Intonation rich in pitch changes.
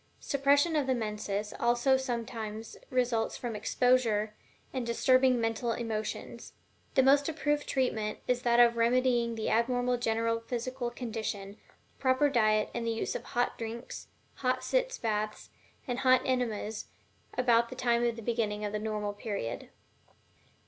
No: narrow, 2.6 semitones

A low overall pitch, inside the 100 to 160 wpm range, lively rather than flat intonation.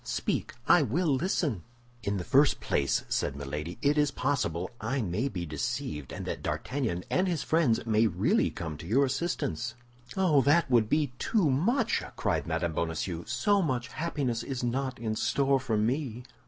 No: low, 125 Hz; average, 170 wpm; wide, 6.1 semitones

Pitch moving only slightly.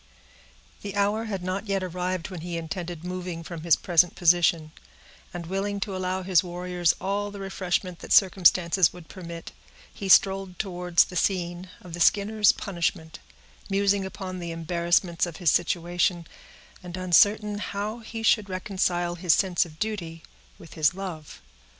Yes: narrow, 2.2 semitones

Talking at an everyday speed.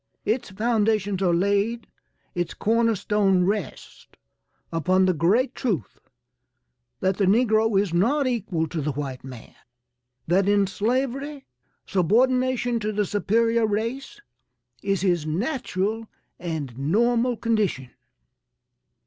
No: slow, 115 wpm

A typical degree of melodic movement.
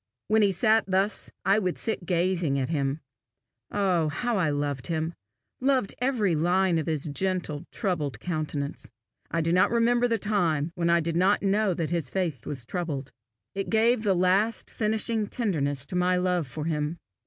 Yes: average, 4.7 semitones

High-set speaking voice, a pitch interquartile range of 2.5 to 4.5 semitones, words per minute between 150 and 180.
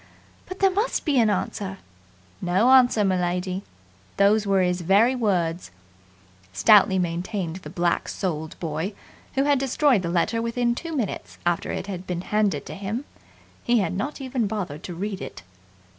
No: high, 195 Hz; average, 4.9 semitones; average, 160 wpm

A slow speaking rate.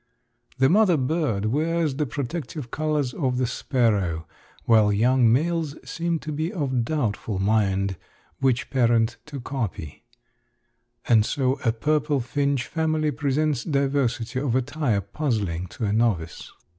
Yes: slow, 130 wpm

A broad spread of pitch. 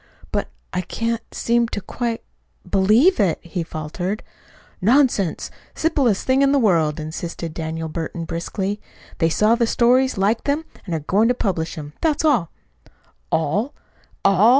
Yes: wide, 6.2 semitones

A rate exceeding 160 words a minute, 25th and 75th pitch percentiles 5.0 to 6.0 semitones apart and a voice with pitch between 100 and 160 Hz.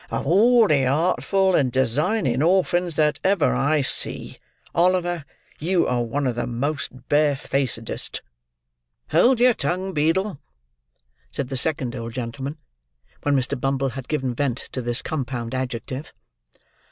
No: average, 140 wpm; average, 5.3 semitones; medium, 140 Hz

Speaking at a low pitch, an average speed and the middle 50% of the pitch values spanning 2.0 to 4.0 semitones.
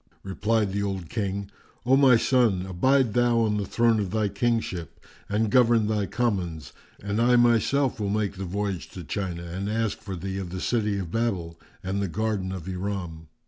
Yes: low, 100 Hz; average, 185 wpm; average, 3.4 semitones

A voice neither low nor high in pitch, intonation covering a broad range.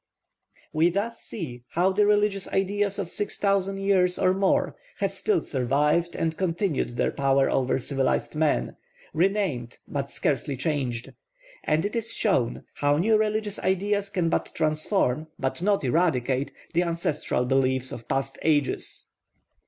Yes: medium, 165 Hz; wide, 6.5 semitones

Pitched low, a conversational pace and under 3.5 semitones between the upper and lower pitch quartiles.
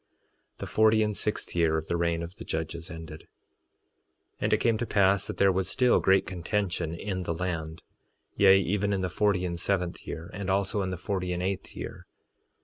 No: very low, 95 Hz; fast, 210 wpm; average, 2.9 semitones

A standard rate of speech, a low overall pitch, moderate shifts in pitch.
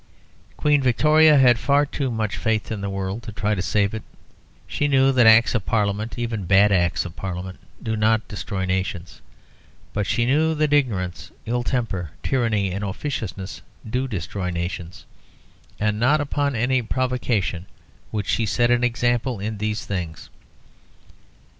Yes: average, 155 wpm; low, 110 Hz; average, 4.5 semitones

